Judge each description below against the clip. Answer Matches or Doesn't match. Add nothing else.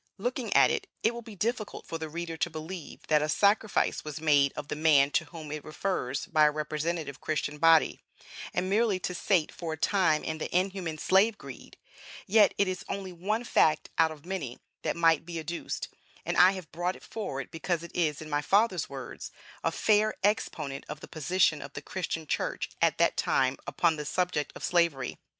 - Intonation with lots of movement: Doesn't match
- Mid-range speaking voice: Matches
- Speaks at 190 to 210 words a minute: Matches